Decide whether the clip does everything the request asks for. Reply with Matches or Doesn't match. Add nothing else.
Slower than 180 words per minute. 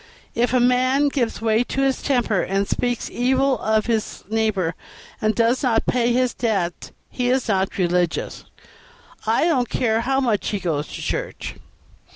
Matches